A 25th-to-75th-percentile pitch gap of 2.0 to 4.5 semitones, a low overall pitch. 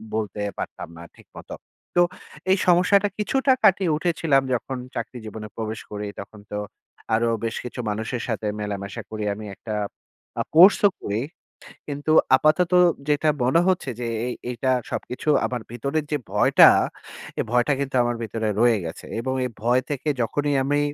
No: wide, 5.6 semitones; low, 125 Hz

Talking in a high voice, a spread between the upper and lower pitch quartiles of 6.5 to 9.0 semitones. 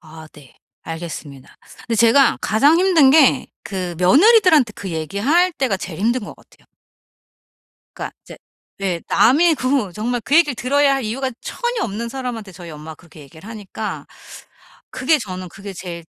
Yes: high, 225 Hz; wide, 7.5 semitones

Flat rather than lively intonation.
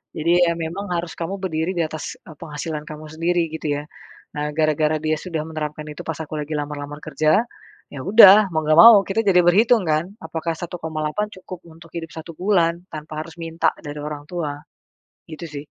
Yes: narrow, 2.1 semitones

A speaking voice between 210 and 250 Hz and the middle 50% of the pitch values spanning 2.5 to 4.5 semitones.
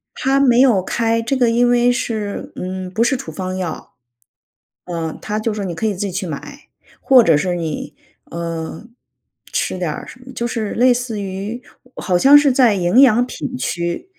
No: high, 215 Hz; average, 5.2 semitones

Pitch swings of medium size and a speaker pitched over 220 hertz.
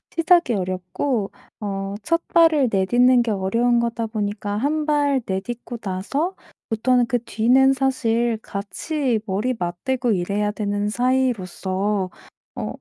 Yes: average, 4.6 semitones; high, 230 Hz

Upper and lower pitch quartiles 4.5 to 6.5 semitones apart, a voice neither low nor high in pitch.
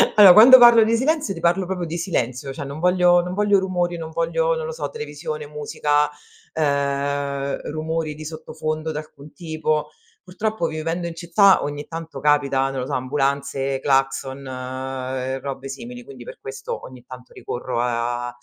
Yes: average, 4.9 semitones; medium, 150 Hz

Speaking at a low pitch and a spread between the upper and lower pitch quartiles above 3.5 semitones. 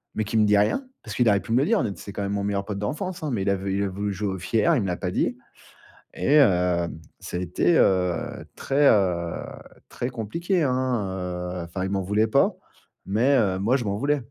Yes: low, 100 Hz; average, 4.4 semitones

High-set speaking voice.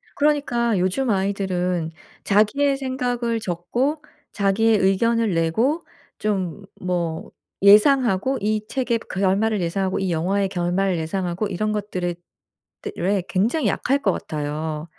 Yes: high, 200 Hz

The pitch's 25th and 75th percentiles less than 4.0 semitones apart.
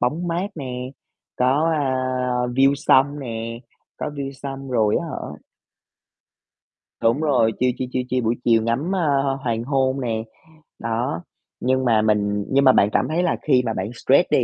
Yes: average, 3.4 semitones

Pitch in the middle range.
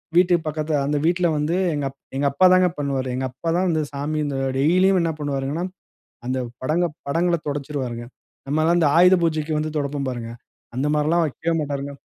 Yes: medium, 150 Hz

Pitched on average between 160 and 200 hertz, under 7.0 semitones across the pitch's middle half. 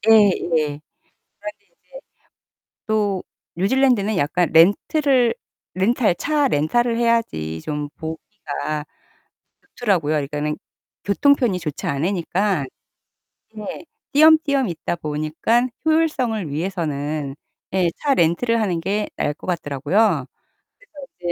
No: high, 190 Hz; wide, 7.4 semitones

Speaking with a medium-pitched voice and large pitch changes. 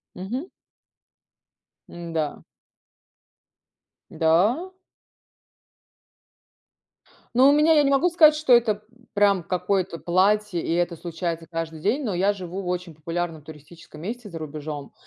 Yes: medium, 180 Hz; wide, 5.9 semitones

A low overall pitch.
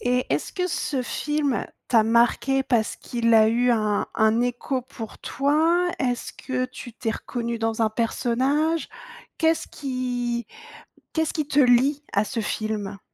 No: high, 245 Hz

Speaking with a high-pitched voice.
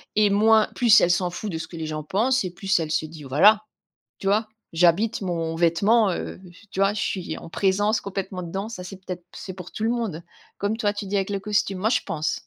Yes: high, 195 Hz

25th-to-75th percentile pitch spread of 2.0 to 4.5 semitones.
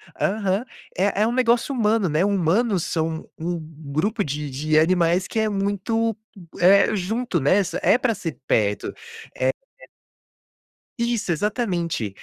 No: wide, 5.6 semitones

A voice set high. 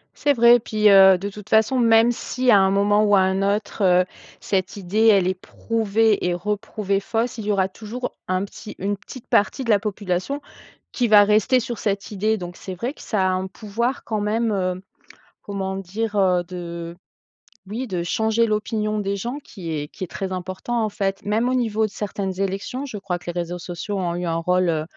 Yes: high, 200 Hz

